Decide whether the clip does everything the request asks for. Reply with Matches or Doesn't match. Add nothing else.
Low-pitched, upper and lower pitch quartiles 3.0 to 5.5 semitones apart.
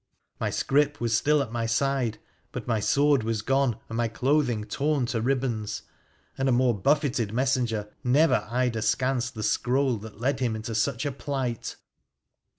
Matches